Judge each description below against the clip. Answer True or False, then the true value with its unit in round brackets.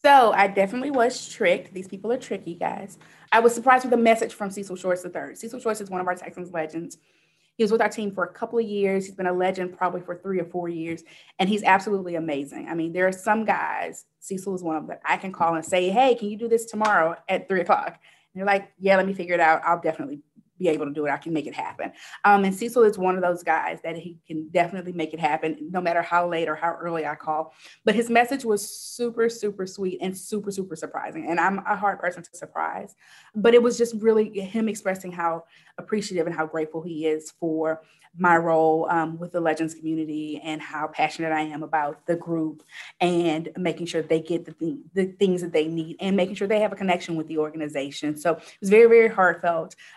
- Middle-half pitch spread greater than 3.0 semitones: True (3.8 semitones)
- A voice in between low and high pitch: True (180 Hz)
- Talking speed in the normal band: False (240 wpm)